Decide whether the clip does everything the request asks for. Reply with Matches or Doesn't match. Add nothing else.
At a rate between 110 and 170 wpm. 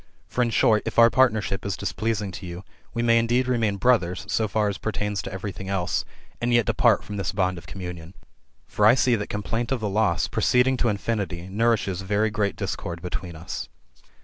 Doesn't match